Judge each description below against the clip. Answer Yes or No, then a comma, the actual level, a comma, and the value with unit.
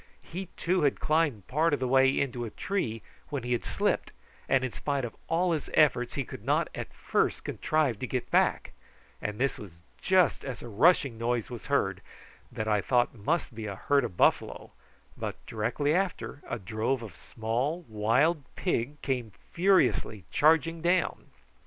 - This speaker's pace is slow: No, average, 175 wpm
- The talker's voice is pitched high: No, low, 130 Hz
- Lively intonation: Yes, wide, 5.7 semitones